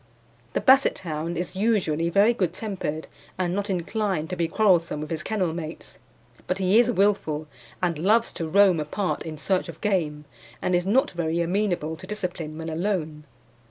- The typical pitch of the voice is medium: Yes, medium, 180 Hz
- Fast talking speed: No, average, 175 wpm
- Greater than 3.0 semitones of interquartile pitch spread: Yes, average, 3.8 semitones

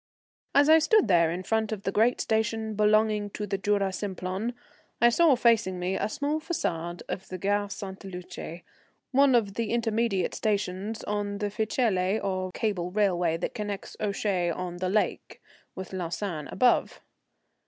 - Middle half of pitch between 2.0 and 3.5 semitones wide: Yes, average, 3.1 semitones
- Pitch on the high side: Yes, high, 205 Hz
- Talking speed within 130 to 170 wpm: Yes, average, 160 wpm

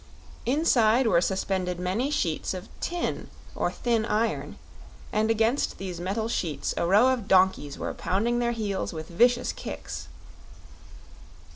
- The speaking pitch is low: No, high, 215 Hz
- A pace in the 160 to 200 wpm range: No, slow, 135 wpm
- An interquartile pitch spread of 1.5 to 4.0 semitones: No, average, 4.6 semitones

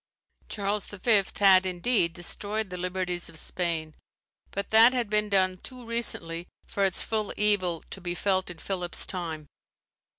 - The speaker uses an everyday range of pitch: Yes, average, 3.0 semitones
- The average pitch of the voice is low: No, high, 190 Hz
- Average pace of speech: Yes, average, 155 wpm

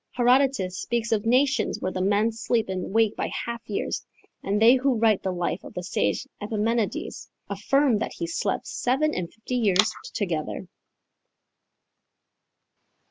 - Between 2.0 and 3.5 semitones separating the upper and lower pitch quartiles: No, average, 4.1 semitones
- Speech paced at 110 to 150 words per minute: Yes, average, 145 wpm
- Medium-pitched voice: No, high, 220 Hz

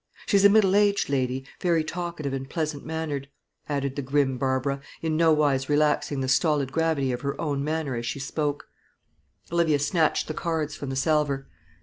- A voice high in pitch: No, medium, 145 Hz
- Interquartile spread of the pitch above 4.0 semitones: No, average, 2.9 semitones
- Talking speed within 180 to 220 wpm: No, average, 170 wpm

